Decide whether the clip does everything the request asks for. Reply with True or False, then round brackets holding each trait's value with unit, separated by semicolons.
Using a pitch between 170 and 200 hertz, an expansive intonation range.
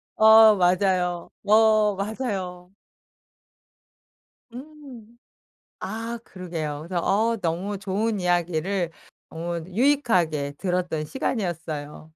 False (190 Hz; 4.1 semitones)